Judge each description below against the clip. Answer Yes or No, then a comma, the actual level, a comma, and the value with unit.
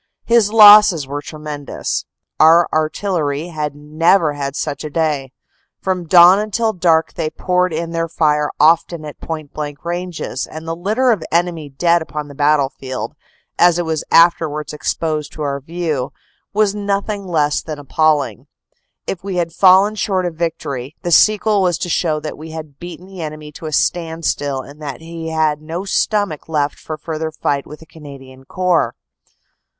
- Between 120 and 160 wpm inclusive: No, average, 170 wpm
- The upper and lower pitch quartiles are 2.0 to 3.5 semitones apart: Yes, average, 3.0 semitones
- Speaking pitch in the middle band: Yes, medium, 160 Hz